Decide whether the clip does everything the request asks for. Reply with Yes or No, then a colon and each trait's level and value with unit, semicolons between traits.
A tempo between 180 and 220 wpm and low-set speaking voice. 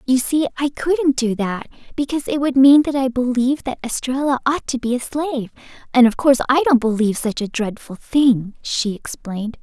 No: average, 200 wpm; very high, 255 Hz